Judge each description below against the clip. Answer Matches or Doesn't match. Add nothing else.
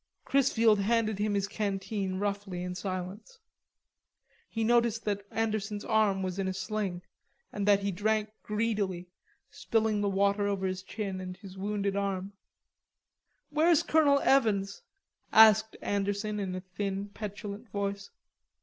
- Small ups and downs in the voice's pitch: Matches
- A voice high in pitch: Matches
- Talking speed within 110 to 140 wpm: Matches